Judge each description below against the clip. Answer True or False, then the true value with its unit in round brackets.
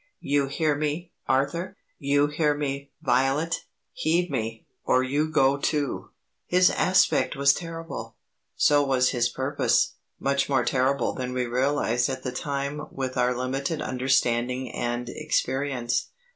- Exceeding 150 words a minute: False (135 wpm)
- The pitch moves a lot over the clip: False (2.6 semitones)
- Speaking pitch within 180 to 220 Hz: False (140 Hz)